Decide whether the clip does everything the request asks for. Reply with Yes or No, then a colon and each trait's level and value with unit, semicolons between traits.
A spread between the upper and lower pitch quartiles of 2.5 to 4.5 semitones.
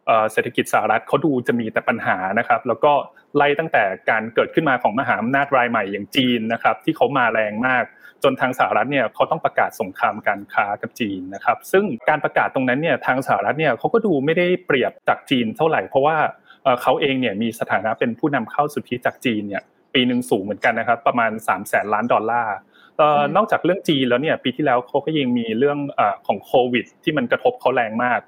No: average, 5.1 semitones